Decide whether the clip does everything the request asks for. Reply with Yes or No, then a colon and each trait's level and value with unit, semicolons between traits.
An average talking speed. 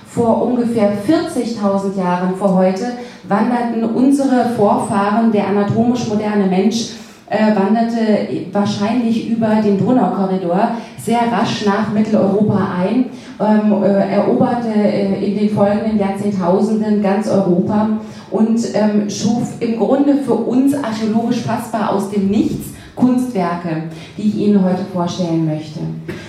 No: slow, 110 wpm